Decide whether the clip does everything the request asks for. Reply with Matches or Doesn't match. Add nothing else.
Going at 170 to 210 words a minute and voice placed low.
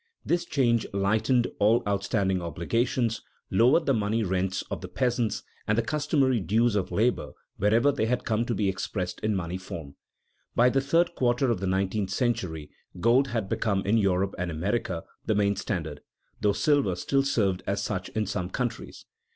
Matches